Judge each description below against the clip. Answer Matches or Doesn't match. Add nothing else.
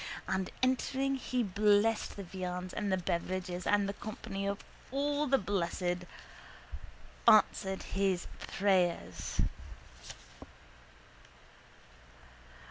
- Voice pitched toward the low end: Doesn't match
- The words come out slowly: Matches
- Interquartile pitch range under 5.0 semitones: Matches